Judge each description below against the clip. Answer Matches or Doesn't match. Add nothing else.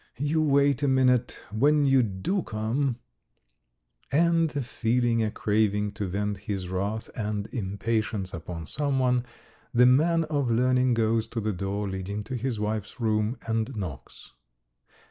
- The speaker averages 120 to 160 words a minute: Matches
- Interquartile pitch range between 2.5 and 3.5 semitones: Doesn't match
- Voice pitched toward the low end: Matches